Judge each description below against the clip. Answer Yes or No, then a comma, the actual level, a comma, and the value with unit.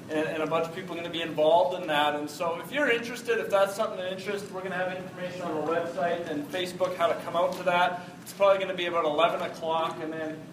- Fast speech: Yes, fast, 275 wpm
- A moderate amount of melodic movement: No, narrow, 2.1 semitones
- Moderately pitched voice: Yes, medium, 175 Hz